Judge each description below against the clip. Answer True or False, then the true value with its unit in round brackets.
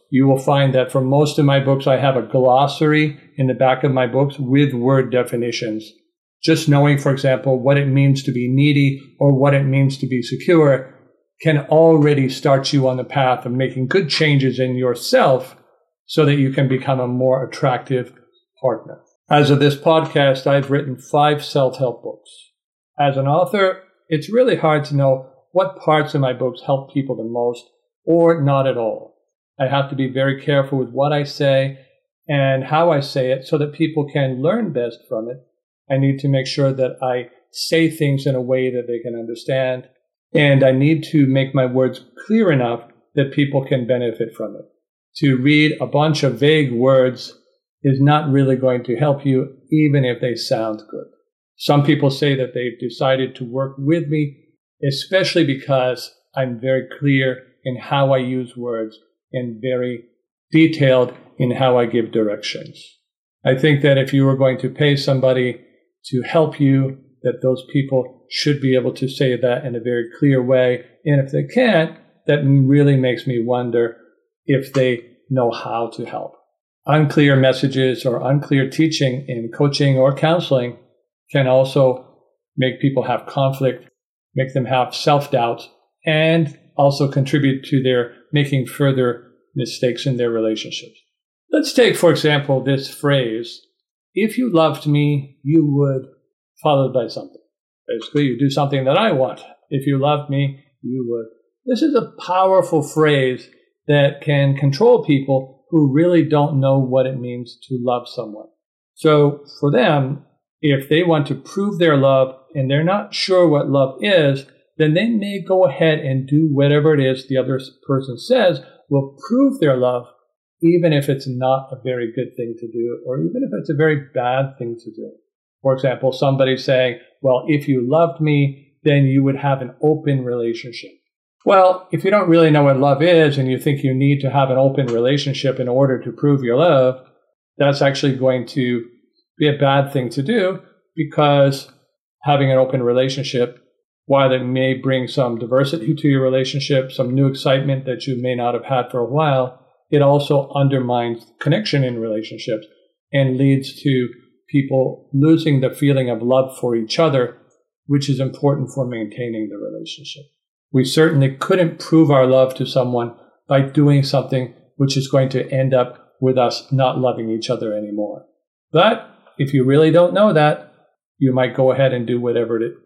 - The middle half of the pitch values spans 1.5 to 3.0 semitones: True (2.5 semitones)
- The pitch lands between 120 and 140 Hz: True (135 Hz)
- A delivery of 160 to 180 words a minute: True (175 wpm)